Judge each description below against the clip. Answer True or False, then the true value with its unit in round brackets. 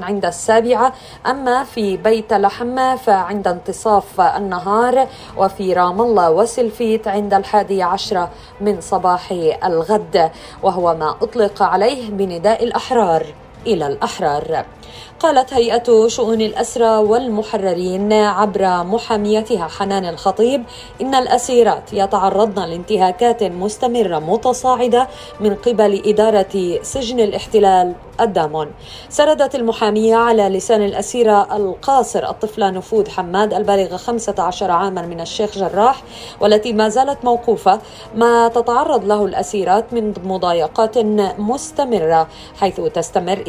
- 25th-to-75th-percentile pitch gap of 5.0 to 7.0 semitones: False (3.4 semitones)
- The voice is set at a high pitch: True (210 Hz)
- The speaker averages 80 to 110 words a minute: True (105 wpm)